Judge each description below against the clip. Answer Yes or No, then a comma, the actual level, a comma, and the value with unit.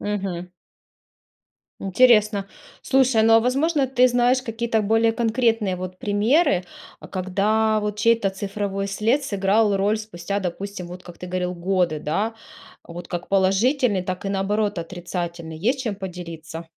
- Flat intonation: No, average, 3.6 semitones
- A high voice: Yes, high, 200 Hz